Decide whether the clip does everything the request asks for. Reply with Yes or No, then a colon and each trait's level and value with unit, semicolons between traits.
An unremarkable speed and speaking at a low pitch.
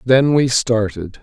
Yes: average, 145 wpm; low, 120 Hz